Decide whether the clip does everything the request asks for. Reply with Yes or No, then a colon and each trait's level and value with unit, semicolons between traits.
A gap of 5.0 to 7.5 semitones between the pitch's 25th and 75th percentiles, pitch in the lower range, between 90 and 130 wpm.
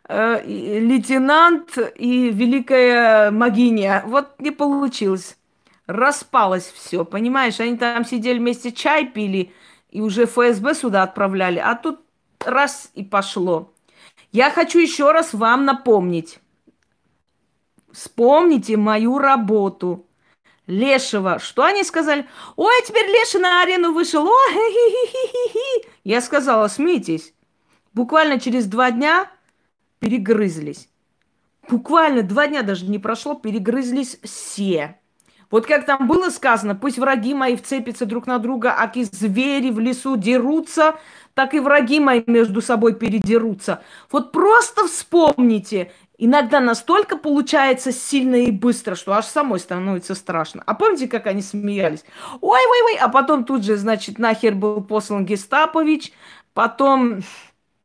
No: wide, 5.4 semitones; high, 245 Hz; average, 120 wpm